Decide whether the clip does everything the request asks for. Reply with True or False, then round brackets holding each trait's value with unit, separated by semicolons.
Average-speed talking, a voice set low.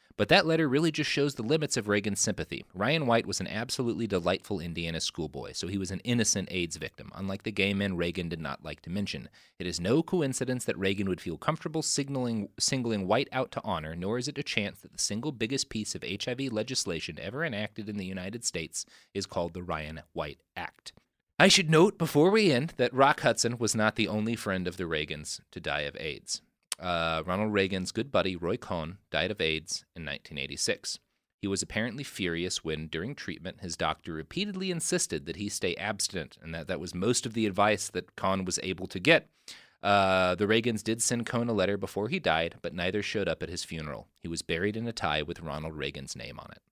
False (215 wpm; 100 Hz)